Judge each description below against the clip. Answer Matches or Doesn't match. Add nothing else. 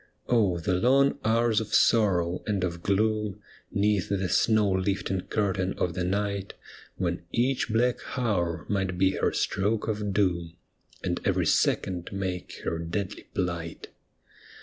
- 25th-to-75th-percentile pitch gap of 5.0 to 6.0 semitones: Doesn't match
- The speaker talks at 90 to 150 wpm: Matches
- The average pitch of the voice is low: Matches